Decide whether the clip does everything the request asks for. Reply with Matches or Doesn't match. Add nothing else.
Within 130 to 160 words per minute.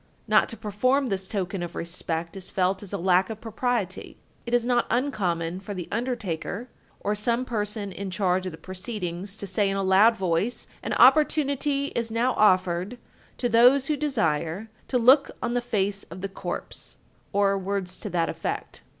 Doesn't match